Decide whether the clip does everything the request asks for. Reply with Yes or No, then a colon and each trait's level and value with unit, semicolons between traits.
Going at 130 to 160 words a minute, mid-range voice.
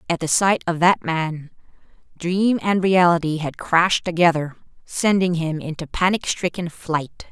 Yes: average, 150 wpm; medium, 170 Hz